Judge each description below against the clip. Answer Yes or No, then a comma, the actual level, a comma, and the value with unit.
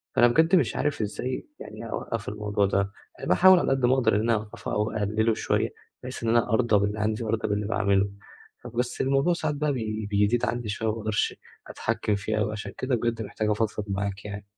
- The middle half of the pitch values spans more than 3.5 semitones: No, average, 2.7 semitones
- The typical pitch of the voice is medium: No, low, 110 Hz